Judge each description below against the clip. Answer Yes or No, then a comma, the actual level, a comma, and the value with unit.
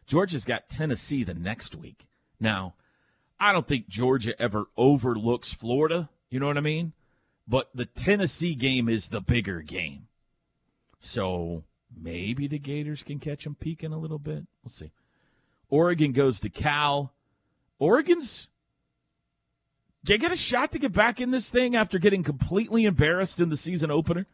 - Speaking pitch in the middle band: Yes, medium, 145 Hz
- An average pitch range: No, wide, 6.0 semitones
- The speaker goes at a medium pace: Yes, average, 155 wpm